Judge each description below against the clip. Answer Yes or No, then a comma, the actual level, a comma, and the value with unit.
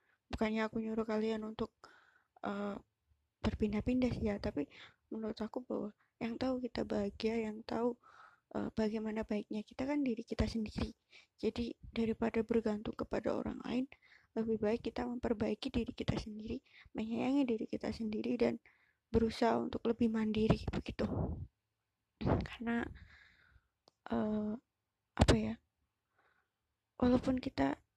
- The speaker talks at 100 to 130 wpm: Yes, average, 120 wpm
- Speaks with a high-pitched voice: Yes, high, 225 Hz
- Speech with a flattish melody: Yes, narrow, 2.0 semitones